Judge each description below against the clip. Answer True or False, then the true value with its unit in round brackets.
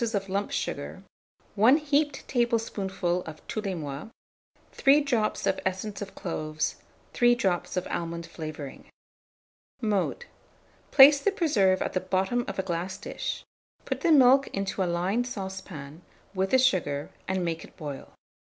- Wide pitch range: True (5.9 semitones)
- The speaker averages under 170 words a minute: True (150 wpm)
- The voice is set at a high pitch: True (195 Hz)